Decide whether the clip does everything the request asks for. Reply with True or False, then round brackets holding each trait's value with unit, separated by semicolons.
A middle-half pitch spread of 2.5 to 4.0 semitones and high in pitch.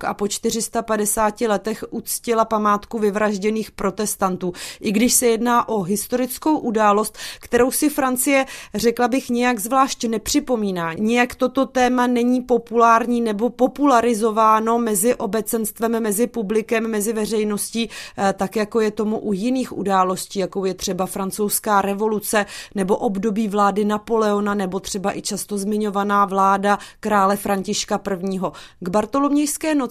True (2.8 semitones; 220 Hz)